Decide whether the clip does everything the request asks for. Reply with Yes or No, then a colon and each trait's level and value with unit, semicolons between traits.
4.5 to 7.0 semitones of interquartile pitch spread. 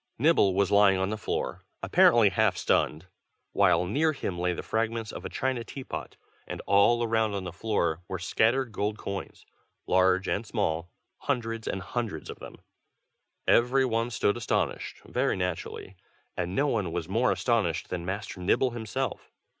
No: average, 4.0 semitones